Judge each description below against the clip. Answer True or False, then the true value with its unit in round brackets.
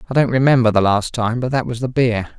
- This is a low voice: True (120 Hz)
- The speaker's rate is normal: False (250 wpm)